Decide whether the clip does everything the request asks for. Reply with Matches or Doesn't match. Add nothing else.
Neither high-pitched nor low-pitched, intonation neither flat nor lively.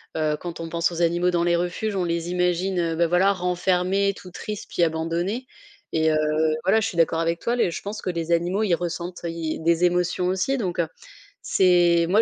Doesn't match